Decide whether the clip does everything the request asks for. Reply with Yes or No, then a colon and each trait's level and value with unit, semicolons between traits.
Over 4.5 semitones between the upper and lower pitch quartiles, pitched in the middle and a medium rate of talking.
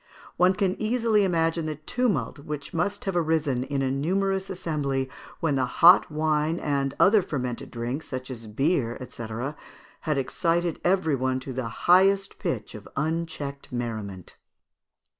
Yes: average, 5.3 semitones; medium, 155 Hz; average, 145 wpm